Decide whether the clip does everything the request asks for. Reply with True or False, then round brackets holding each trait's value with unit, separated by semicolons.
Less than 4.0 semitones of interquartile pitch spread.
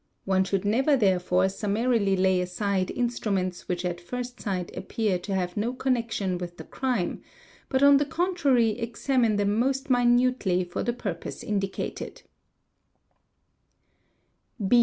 False (5.0 semitones)